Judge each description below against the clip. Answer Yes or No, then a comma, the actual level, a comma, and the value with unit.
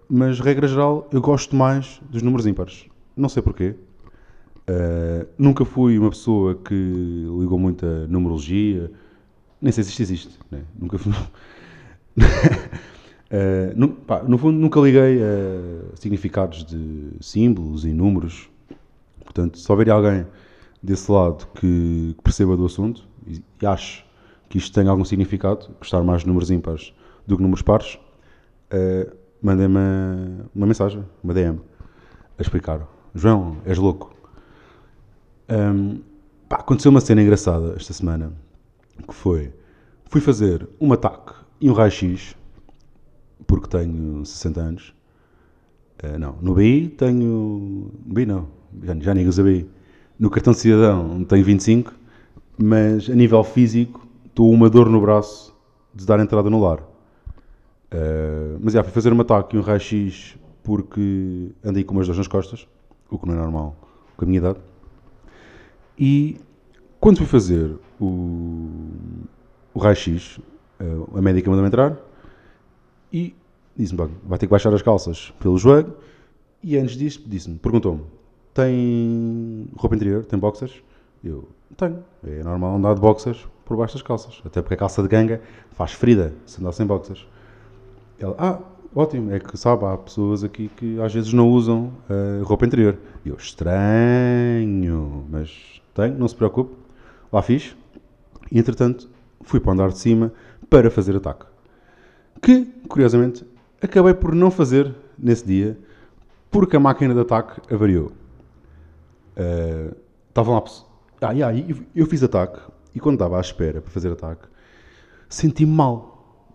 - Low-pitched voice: Yes, low, 105 Hz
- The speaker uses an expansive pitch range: No, average, 4.7 semitones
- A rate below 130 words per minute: No, average, 150 wpm